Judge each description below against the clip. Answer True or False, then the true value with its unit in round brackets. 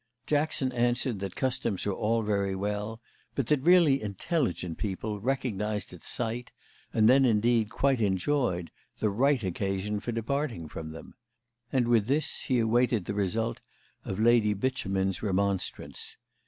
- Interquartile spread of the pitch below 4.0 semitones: False (4.3 semitones)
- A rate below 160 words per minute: True (140 wpm)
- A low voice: True (110 Hz)